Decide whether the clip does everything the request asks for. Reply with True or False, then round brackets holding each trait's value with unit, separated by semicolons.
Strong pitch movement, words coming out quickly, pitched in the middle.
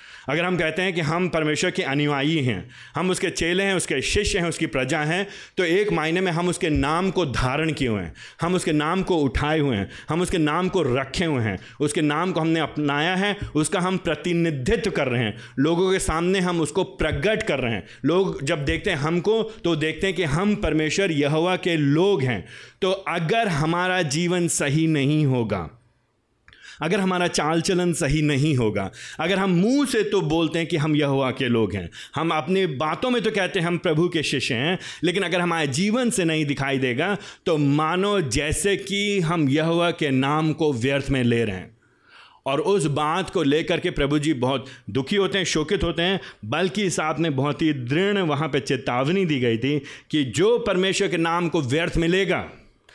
False (4.2 semitones; 205 wpm; 165 Hz)